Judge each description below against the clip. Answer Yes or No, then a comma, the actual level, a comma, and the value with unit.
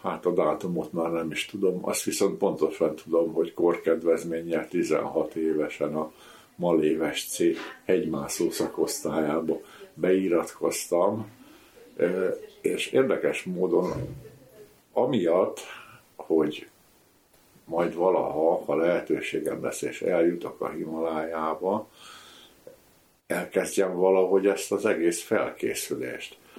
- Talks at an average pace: No, slow, 90 wpm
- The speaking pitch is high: No, very low, 85 Hz